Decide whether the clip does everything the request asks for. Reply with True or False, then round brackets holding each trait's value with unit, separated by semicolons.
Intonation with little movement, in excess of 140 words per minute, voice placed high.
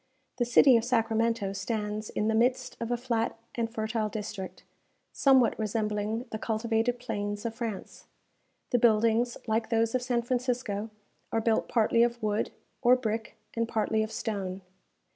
True (1.8 semitones; 155 wpm; 225 Hz)